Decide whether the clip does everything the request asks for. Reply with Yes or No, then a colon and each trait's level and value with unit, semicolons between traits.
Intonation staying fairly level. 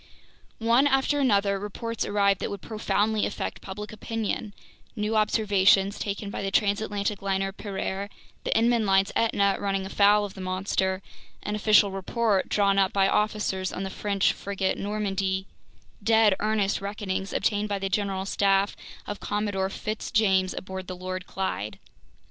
Yes: narrow, 1.6 semitones